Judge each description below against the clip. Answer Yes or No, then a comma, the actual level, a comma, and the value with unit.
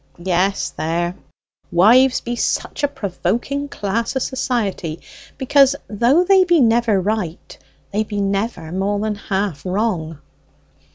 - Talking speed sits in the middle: No, slow, 125 wpm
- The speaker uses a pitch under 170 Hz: No, high, 210 Hz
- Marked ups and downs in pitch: No, average, 5.0 semitones